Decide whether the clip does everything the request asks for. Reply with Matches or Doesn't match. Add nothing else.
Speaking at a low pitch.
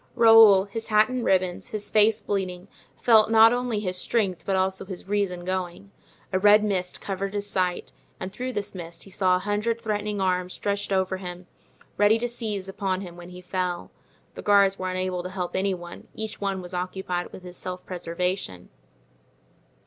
Doesn't match